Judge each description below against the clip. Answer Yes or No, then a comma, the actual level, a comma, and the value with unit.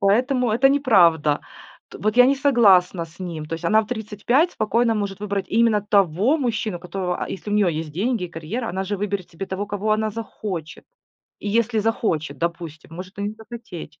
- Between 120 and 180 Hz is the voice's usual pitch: No, high, 205 Hz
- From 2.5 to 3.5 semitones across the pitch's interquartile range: No, average, 4.2 semitones